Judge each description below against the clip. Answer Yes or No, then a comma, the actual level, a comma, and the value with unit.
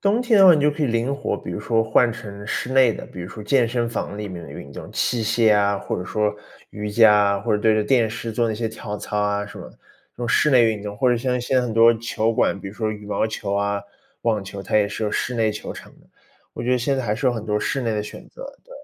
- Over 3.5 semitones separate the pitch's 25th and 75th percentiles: No, average, 2.7 semitones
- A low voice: Yes, low, 110 Hz